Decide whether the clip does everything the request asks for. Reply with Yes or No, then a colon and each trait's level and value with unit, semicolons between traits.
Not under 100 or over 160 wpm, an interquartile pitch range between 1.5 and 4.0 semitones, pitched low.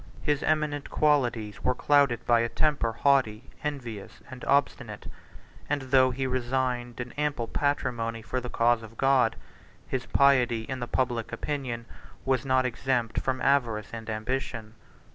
Yes: average, 145 wpm; average, 2.8 semitones; low, 125 Hz